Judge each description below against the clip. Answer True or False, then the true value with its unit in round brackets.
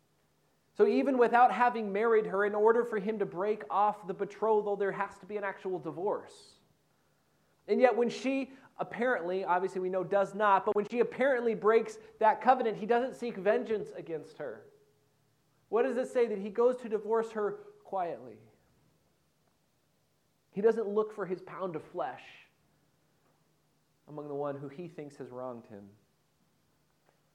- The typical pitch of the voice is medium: False (210 Hz)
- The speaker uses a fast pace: False (160 wpm)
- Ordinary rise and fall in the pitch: True (3.9 semitones)